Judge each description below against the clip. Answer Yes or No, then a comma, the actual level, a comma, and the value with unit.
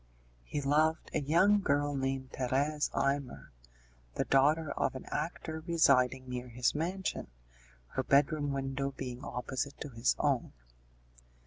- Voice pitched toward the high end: No, medium, 140 Hz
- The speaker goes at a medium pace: No, slow, 130 wpm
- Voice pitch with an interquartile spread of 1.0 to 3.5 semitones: Yes, average, 2.7 semitones